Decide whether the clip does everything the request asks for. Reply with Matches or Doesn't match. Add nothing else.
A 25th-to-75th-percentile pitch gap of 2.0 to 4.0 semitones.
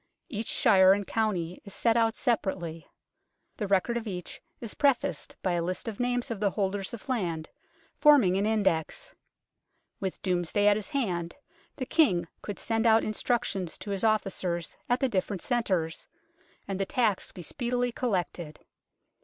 Doesn't match